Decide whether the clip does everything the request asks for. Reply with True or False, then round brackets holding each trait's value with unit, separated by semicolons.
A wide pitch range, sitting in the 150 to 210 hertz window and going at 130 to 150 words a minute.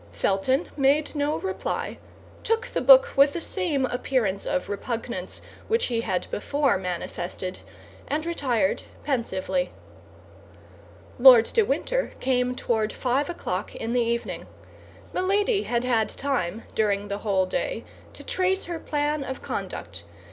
False (6.0 semitones; 260 Hz; 135 wpm)